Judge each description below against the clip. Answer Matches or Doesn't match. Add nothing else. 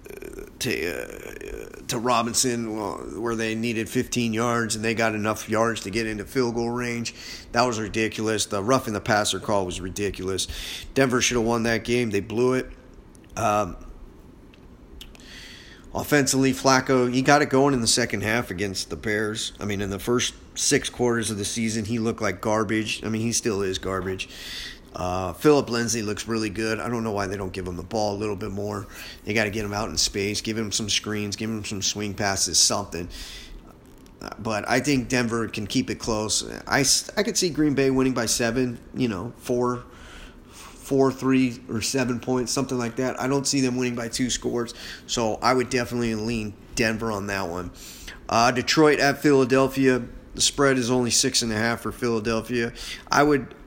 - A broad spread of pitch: Doesn't match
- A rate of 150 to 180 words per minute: Doesn't match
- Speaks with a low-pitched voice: Matches